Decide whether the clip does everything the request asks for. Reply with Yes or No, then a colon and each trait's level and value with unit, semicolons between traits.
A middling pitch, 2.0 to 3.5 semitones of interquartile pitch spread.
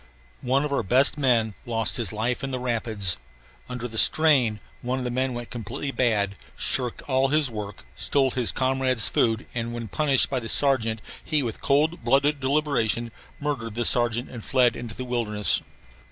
No: low, 125 Hz; average, 3.0 semitones